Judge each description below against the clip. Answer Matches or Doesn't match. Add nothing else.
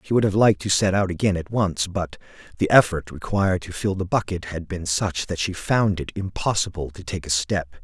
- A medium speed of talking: Doesn't match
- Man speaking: Matches